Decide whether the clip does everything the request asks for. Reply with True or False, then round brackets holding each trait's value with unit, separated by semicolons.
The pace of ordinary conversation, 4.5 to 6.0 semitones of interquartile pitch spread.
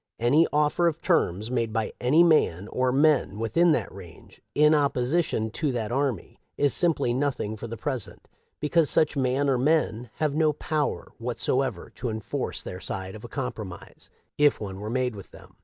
True (180 wpm; 5.3 semitones)